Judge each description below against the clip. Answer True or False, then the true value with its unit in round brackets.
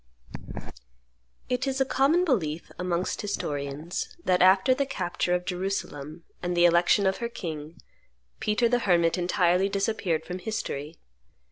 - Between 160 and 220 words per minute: False (135 wpm)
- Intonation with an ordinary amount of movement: True (4.2 semitones)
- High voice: False (180 Hz)